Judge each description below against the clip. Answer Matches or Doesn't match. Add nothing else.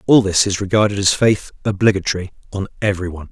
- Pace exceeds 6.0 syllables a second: Matches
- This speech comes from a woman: Doesn't match